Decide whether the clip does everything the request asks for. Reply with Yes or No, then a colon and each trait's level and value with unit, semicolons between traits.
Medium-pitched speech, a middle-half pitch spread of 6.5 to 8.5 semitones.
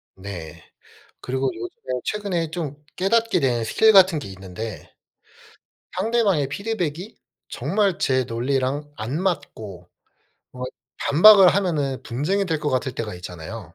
Yes: medium, 145 Hz; wide, 8.2 semitones